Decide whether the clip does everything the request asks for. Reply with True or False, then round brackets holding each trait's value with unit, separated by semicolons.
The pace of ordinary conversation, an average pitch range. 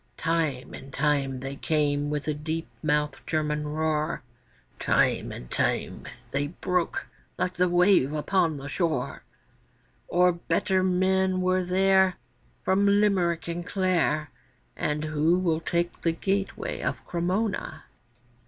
False (125 wpm; 3.6 semitones)